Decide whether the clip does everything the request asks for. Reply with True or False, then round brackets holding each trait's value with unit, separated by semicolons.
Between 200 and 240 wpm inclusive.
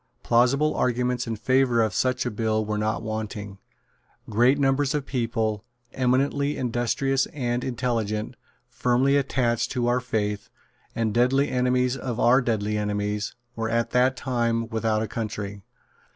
False (140 wpm)